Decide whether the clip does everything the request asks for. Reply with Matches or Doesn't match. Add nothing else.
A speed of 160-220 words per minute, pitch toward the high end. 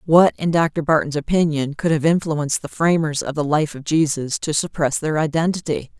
Doesn't match